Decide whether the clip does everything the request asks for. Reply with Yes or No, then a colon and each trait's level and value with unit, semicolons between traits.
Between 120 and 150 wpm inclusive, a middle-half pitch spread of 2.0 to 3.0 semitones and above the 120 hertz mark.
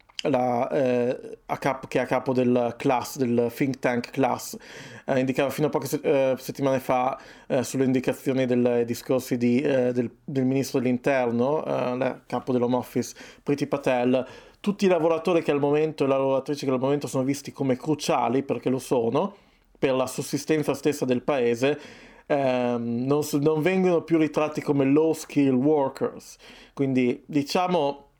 No: average, 165 wpm; average, 2.7 semitones; low, 135 Hz